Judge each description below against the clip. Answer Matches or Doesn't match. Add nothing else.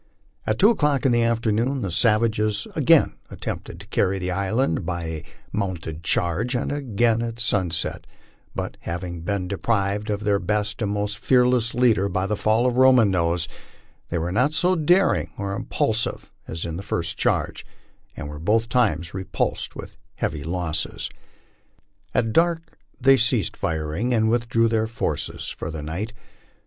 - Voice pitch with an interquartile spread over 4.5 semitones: Matches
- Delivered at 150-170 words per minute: Matches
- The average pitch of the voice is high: Doesn't match